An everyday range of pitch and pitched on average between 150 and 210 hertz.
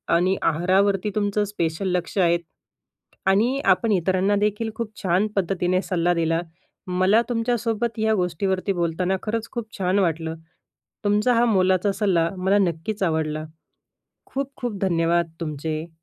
Yes: average, 3.6 semitones; high, 190 Hz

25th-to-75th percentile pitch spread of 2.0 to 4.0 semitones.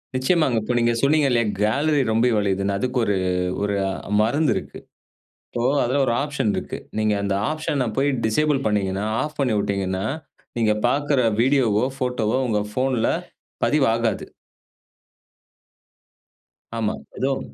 No: average, 4.6 semitones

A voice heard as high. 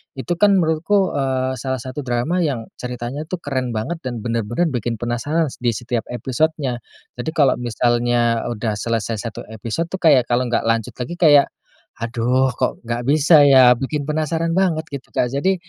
No: low, 130 Hz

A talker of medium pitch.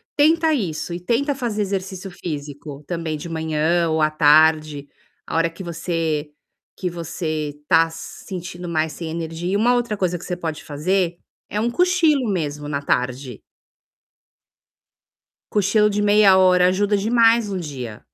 Yes: medium, 175 Hz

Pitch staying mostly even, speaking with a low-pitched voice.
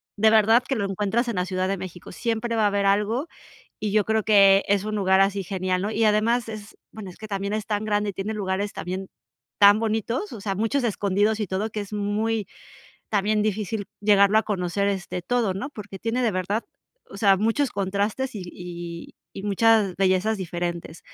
No: narrow, 2.2 semitones; high, 205 Hz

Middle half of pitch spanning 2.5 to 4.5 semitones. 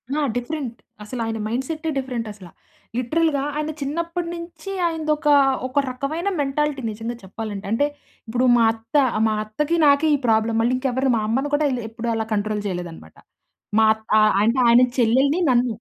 No: average, 5.0 semitones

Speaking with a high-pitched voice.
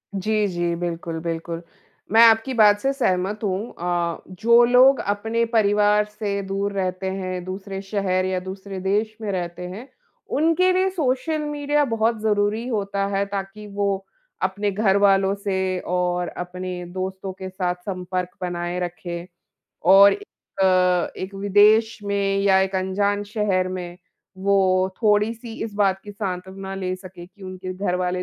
Yes: high, 195 Hz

